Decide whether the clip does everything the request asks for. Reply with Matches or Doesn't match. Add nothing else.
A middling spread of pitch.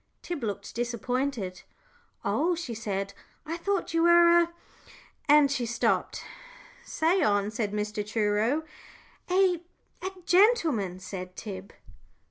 Doesn't match